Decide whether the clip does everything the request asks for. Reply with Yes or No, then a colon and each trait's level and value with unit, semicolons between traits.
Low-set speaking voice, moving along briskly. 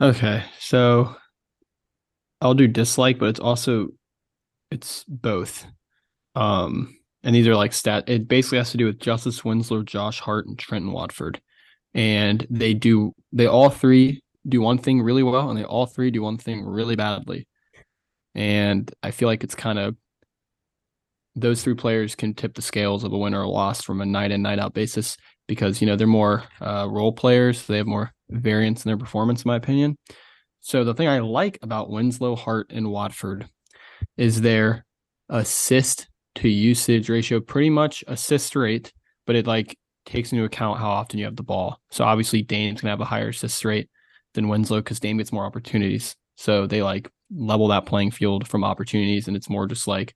No: low, 110 Hz; average, 185 wpm